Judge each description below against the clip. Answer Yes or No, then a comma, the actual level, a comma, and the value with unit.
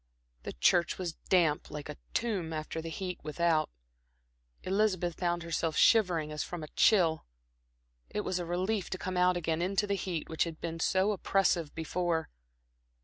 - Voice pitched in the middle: Yes, medium, 175 Hz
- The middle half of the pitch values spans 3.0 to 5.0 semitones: No, narrow, 2.6 semitones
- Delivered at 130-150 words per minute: No, average, 165 wpm